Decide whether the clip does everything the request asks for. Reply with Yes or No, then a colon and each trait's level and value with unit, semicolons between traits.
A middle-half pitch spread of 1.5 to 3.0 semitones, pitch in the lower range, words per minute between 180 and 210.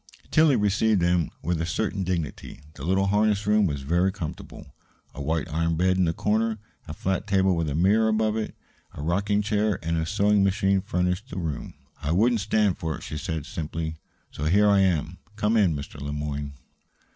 No: average, 4.3 semitones; very low, 95 Hz; average, 195 wpm